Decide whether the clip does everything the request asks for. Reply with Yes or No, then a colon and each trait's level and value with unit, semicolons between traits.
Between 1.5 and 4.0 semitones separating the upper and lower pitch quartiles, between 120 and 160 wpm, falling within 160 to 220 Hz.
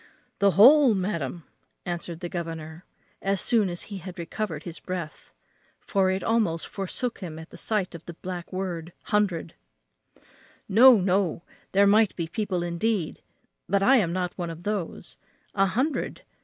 Yes: average, 3.3 semitones; average, 155 wpm; medium, 185 Hz